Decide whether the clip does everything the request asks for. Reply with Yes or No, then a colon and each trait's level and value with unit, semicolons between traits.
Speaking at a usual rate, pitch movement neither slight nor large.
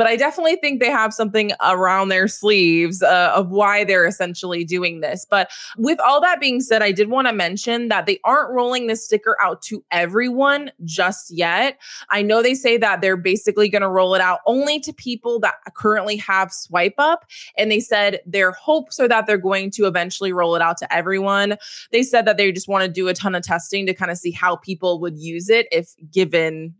No: fast, 220 wpm; average, 4.3 semitones